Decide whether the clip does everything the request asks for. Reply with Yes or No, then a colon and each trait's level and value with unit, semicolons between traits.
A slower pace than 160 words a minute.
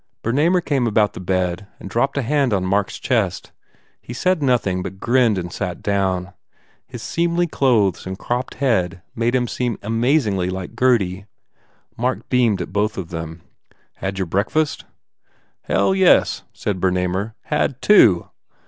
Yes: average, 150 wpm